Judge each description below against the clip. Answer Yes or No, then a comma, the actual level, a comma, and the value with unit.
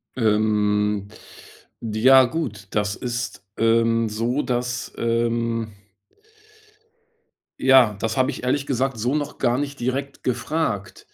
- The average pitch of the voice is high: No, low, 120 Hz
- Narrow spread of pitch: No, average, 3.1 semitones